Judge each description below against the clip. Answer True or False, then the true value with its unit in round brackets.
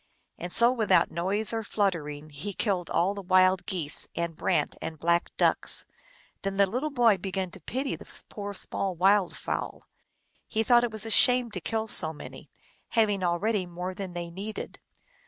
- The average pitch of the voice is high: True (195 Hz)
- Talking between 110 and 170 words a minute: False (180 wpm)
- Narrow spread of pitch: False (3.8 semitones)